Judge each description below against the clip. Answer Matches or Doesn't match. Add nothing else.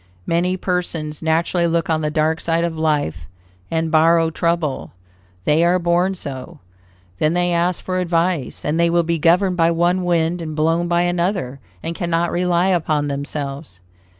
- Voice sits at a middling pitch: Matches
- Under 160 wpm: Doesn't match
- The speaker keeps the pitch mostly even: Matches